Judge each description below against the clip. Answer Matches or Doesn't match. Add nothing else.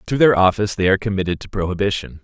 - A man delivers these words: Matches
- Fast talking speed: Matches